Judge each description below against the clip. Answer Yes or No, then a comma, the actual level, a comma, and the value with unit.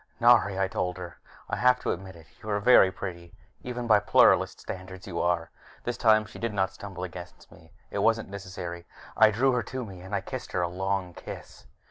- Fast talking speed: Yes, fast, 215 wpm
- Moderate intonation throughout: Yes, average, 3.4 semitones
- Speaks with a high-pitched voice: No, very low, 95 Hz